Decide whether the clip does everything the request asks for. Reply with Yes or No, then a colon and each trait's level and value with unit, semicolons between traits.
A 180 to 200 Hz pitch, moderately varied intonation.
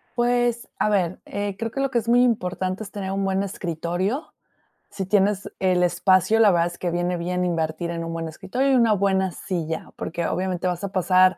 Yes: high, 190 Hz; average, 3.1 semitones